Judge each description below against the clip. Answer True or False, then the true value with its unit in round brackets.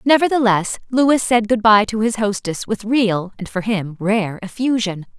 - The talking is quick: False (175 wpm)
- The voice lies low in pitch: False (215 Hz)